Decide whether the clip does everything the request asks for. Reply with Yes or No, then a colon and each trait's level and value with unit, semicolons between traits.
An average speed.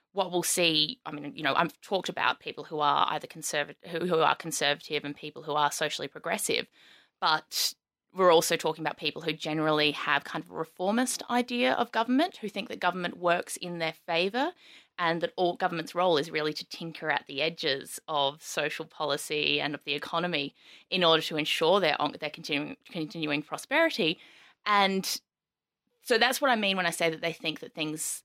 Yes: average, 195 wpm